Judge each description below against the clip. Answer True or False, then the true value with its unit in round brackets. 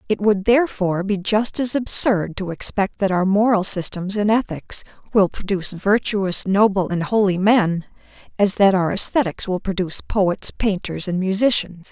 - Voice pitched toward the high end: True (195 Hz)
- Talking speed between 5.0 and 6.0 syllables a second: False (4.8 syllables/s)